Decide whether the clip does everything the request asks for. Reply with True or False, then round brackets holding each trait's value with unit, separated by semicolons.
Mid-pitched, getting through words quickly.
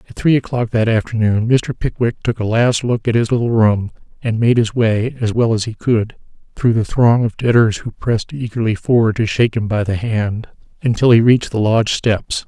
False (115 Hz; 215 wpm)